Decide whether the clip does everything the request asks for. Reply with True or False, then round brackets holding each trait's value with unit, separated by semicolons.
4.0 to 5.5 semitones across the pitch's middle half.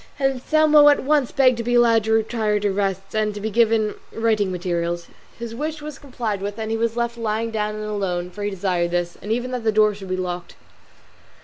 False (3.2 semitones)